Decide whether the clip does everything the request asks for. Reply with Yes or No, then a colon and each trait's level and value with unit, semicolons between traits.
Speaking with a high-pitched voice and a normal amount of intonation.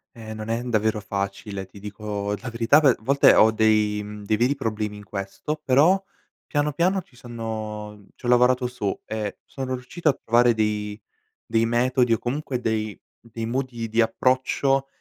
No: low, 115 Hz; average, 3.2 semitones